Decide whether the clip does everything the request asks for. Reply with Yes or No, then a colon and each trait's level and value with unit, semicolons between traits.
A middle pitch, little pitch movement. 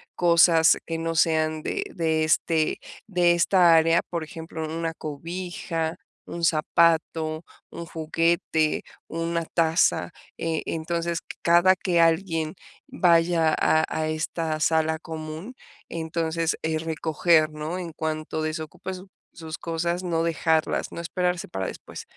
Yes: medium, 165 Hz; narrow, 1.2 semitones